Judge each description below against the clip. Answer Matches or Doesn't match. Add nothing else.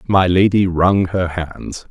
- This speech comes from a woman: Doesn't match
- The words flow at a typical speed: Matches